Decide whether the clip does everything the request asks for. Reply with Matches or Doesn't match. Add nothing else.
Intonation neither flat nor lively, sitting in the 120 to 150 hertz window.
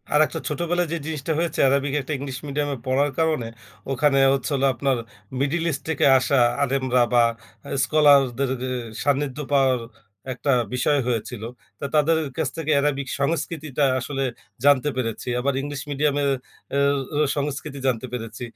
Doesn't match